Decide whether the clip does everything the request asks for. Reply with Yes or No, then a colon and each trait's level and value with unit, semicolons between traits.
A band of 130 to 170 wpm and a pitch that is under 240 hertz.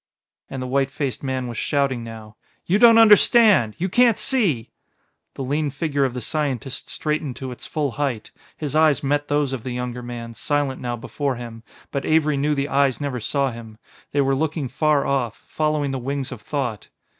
No: average, 195 wpm; medium, 140 Hz